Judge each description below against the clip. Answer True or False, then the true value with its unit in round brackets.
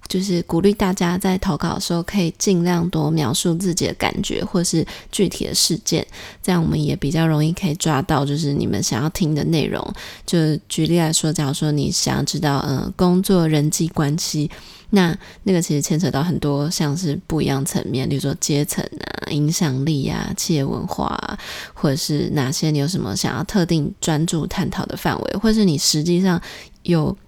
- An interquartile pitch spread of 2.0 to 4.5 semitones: True (3.0 semitones)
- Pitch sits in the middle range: True (160 Hz)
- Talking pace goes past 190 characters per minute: True (295 characters per minute)